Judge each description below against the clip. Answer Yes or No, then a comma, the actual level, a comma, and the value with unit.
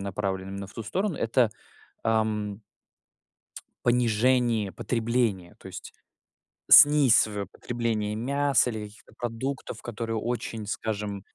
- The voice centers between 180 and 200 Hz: No, low, 115 Hz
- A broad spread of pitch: No, narrow, 2.6 semitones